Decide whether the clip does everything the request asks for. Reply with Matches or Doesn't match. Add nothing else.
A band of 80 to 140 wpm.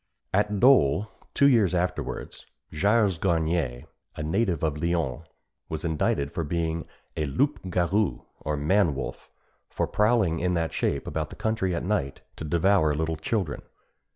Doesn't match